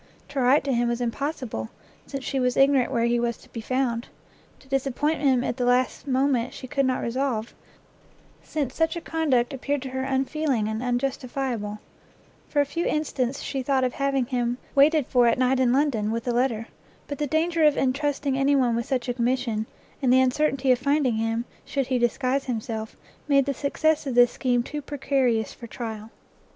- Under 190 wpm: No, average, 195 wpm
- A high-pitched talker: Yes, very high, 260 Hz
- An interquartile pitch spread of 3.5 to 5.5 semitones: No, narrow, 2.6 semitones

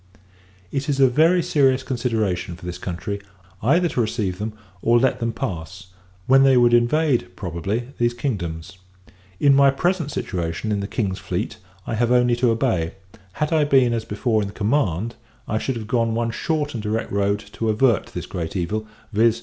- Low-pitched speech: Yes, low, 115 Hz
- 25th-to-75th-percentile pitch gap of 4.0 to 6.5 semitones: Yes, average, 4.8 semitones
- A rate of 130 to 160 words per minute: No, average, 185 wpm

